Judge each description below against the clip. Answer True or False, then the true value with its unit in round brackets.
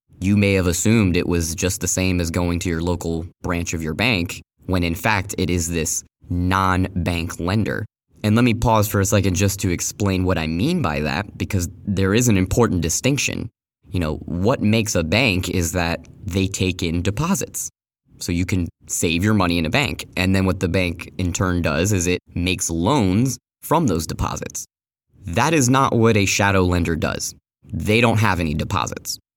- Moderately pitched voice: False (95 Hz)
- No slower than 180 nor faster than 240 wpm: True (200 wpm)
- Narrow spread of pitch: False (3.3 semitones)